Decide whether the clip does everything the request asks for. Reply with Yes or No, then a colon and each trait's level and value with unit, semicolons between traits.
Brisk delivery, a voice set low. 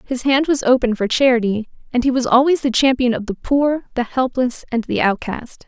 No: fast, 210 wpm; very high, 250 Hz